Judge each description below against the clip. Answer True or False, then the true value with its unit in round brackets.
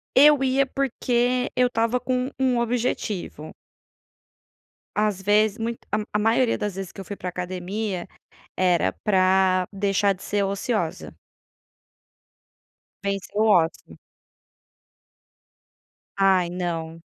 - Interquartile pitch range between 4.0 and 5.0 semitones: True (4.3 semitones)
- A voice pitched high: True (205 Hz)